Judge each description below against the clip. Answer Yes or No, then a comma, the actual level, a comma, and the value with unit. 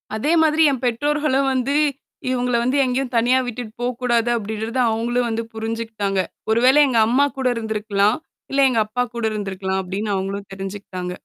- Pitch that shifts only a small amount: No, average, 3.5 semitones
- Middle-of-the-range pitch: No, high, 230 Hz